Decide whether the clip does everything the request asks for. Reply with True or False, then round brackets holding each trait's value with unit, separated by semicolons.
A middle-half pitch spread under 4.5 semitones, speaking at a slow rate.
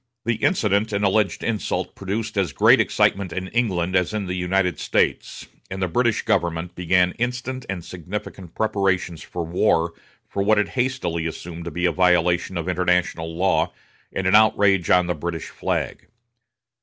False (3.1 semitones; 165 wpm)